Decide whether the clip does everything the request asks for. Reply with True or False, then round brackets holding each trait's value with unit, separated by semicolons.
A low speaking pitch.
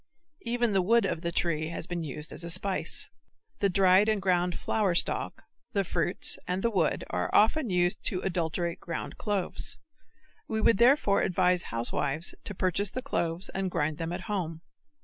False (180 Hz)